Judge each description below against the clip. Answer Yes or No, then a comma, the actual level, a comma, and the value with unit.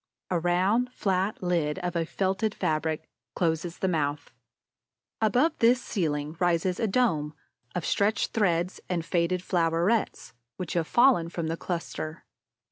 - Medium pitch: Yes, medium, 175 Hz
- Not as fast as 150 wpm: Yes, slow, 135 wpm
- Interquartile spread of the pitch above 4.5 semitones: No, average, 3.2 semitones